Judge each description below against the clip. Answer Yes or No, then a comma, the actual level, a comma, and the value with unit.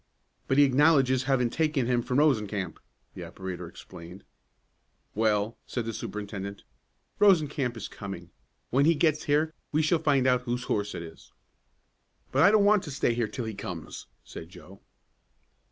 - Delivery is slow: No, average, 160 wpm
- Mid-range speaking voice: No, low, 125 Hz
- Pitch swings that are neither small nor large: No, wide, 6.2 semitones